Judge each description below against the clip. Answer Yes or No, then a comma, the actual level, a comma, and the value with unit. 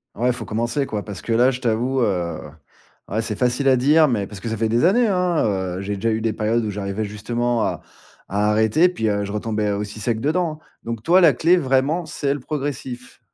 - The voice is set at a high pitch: No, low, 115 Hz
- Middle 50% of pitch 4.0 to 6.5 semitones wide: Yes, average, 4.7 semitones